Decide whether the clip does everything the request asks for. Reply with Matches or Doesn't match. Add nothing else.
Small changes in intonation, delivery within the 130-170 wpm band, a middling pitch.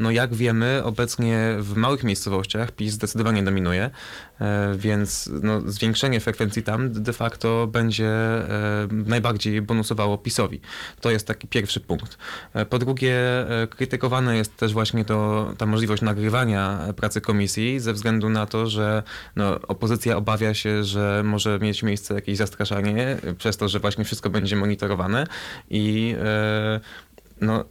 Doesn't match